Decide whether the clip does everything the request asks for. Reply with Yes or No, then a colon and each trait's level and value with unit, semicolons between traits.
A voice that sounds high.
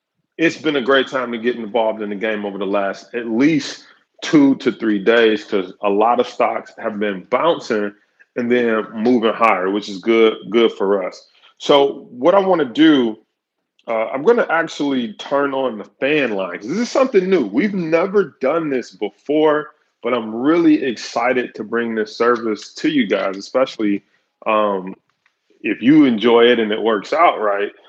No: low, 120 Hz